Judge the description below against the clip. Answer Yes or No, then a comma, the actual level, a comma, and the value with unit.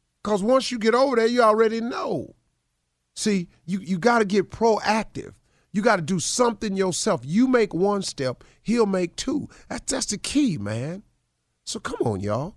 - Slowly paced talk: No, average, 180 wpm